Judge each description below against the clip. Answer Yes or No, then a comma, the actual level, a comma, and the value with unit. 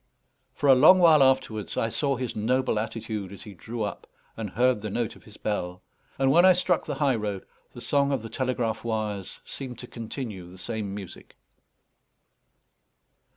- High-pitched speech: No, low, 115 Hz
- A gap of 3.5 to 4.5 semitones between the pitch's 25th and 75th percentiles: Yes, average, 4.1 semitones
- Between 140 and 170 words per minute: No, average, 180 wpm